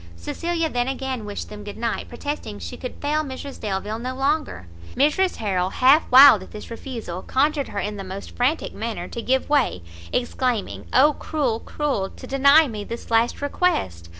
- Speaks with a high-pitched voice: Yes, very high, 250 Hz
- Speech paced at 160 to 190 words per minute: Yes, average, 175 wpm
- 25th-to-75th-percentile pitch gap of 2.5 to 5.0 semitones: No, wide, 5.5 semitones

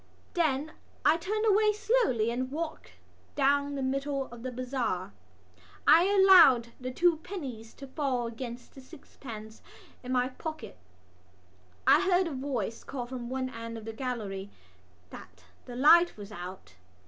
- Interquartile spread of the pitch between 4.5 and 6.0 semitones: Yes, average, 5.2 semitones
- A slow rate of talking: No, average, 150 wpm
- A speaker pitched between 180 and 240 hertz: No, very high, 260 Hz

